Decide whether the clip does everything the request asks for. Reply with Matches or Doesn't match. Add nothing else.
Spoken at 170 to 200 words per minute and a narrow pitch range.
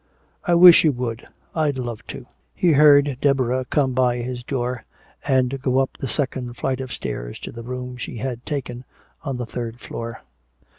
Matches